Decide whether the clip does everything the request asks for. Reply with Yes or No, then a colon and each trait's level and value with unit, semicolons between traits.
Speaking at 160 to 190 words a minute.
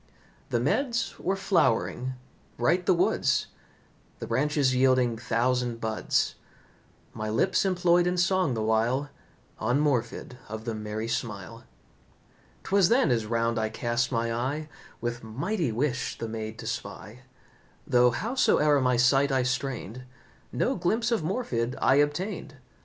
No: slow, 135 wpm